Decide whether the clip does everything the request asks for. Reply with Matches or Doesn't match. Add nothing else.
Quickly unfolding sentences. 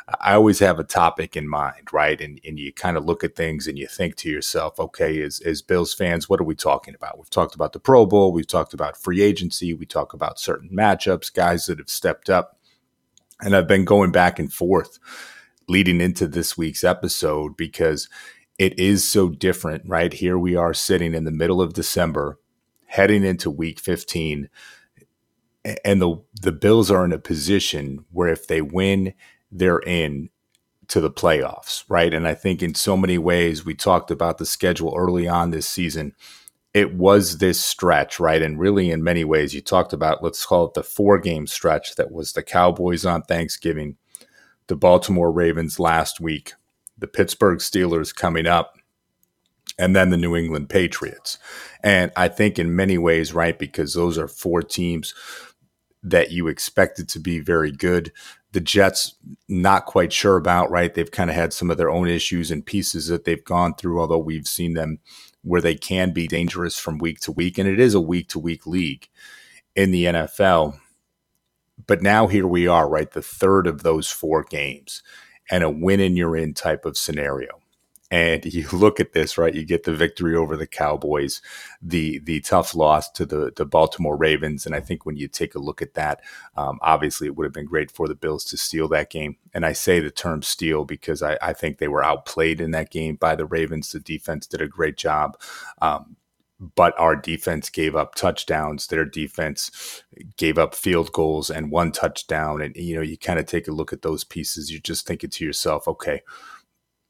Doesn't match